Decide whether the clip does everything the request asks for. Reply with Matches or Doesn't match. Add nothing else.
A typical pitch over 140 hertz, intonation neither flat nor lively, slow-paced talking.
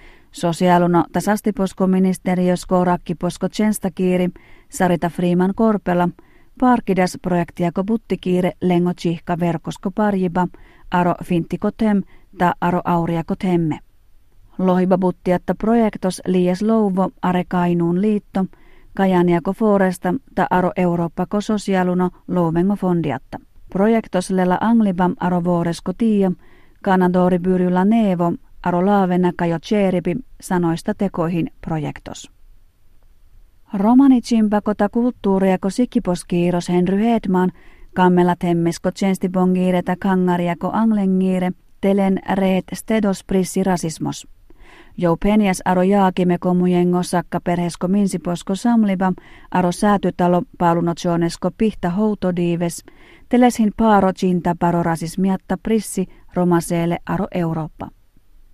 Doesn't match